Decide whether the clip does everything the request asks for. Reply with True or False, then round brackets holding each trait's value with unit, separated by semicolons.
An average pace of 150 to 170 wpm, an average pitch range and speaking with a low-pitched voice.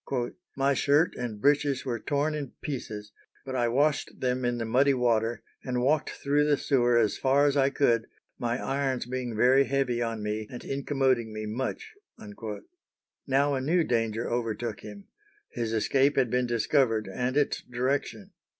True (165 wpm; 3.1 semitones; 125 Hz)